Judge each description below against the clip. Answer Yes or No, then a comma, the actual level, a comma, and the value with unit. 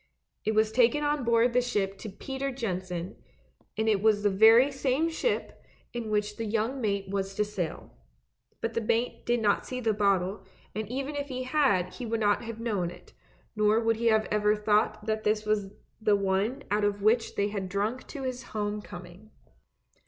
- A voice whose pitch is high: Yes, high, 215 Hz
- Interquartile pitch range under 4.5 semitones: Yes, average, 2.8 semitones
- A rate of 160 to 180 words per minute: No, average, 195 wpm